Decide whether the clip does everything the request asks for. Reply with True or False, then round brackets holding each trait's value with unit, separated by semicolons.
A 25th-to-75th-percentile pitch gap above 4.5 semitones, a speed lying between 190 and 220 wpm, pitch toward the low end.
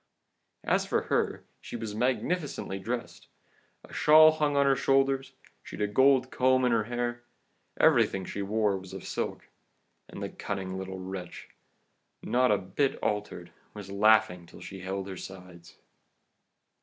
False (5.3 semitones; 150 wpm; 105 Hz)